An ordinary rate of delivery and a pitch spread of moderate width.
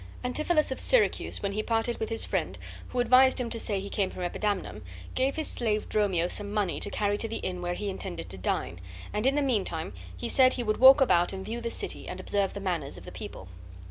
No: fast, 240 wpm; average, 4.9 semitones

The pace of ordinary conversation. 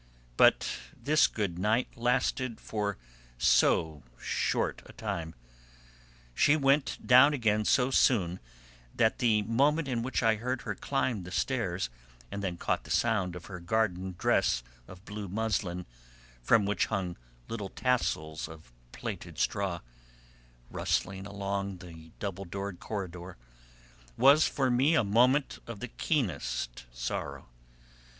No: slow, 130 wpm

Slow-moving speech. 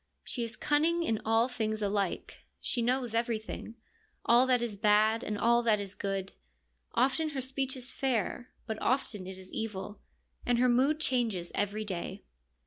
No: average, 165 wpm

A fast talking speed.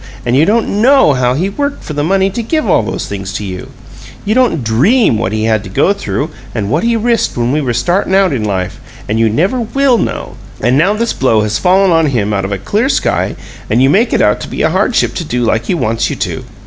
Yes: fast, 255 wpm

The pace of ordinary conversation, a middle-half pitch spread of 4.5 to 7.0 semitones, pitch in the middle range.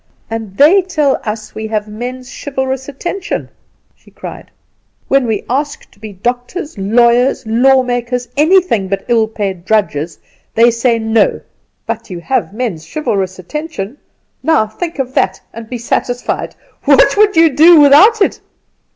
No: average, 150 wpm; average, 4.9 semitones; high, 245 Hz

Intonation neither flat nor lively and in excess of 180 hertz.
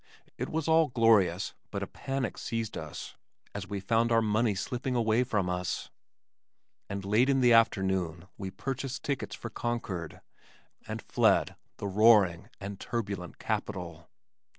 No: average, 3.9 semitones; low, 110 Hz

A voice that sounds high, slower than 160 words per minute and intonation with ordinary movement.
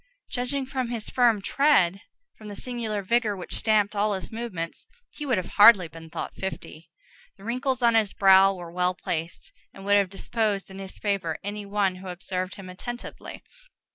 No: high, 200 Hz; average, 180 wpm; average, 4.0 semitones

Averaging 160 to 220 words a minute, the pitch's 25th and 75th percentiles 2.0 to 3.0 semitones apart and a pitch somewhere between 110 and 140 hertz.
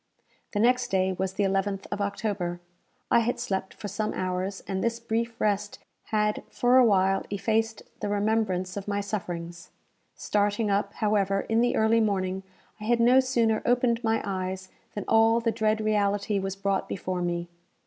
No: average, 170 wpm; average, 2.7 semitones; high, 205 Hz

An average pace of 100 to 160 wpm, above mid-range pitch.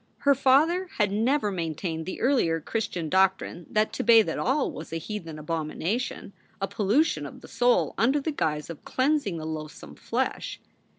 No: average, 175 wpm; high, 200 Hz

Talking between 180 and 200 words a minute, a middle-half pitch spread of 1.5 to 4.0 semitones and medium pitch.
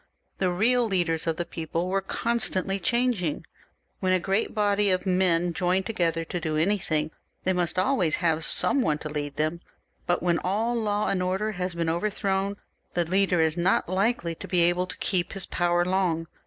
Yes: average, 185 wpm; average, 2.7 semitones; medium, 180 Hz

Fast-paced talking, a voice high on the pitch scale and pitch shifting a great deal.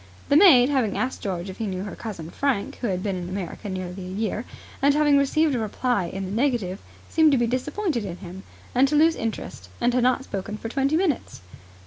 Yes: fast, 225 wpm; high, 230 Hz; wide, 6.4 semitones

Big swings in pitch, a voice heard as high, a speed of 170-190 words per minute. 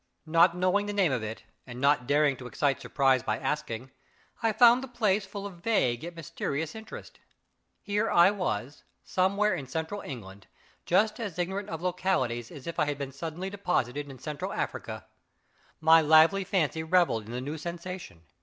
No: wide, 6.0 semitones; medium, 165 Hz; average, 175 wpm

